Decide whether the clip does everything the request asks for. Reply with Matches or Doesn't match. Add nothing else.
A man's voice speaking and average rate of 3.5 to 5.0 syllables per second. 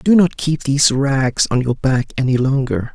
Matches